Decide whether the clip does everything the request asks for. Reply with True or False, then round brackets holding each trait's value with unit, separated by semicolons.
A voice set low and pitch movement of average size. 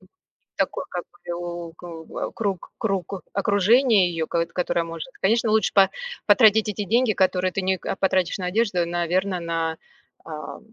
False (185 Hz; 3.2 semitones)